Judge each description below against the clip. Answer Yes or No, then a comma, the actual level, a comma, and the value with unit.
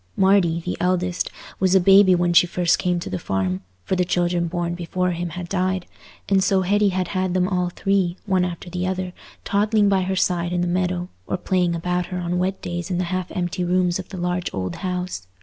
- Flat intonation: Yes, narrow, 1.1 semitones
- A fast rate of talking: Yes, fast, 220 wpm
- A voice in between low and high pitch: Yes, medium, 180 Hz